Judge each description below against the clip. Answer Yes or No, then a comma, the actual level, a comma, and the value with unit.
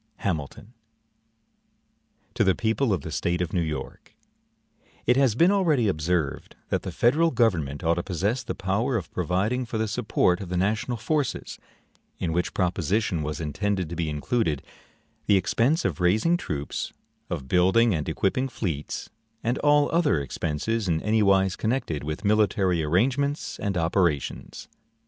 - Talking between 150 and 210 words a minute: Yes, average, 155 wpm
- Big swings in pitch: Yes, wide, 5.9 semitones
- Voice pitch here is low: Yes, very low, 95 Hz